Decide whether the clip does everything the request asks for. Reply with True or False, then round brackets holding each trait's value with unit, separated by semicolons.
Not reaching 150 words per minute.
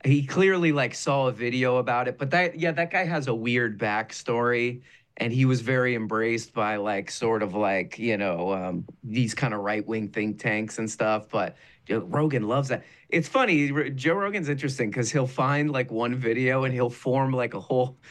False (200 wpm)